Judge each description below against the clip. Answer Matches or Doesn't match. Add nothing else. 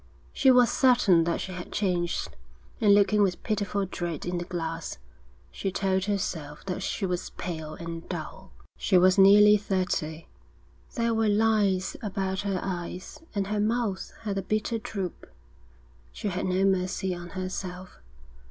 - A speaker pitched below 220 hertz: Matches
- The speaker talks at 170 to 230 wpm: Doesn't match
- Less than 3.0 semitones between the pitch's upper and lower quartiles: Matches